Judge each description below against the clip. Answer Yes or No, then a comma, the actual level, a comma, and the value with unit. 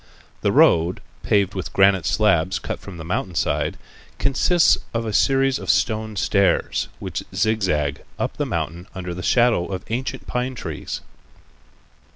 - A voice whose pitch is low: Yes, low, 100 Hz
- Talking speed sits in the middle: Yes, average, 155 wpm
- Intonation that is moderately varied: Yes, average, 4.9 semitones